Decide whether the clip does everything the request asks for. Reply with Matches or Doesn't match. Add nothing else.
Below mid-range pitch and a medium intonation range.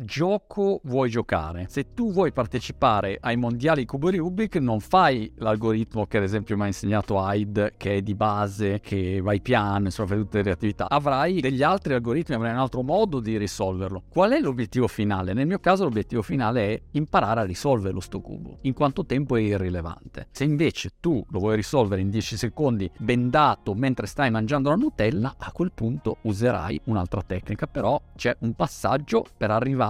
Matches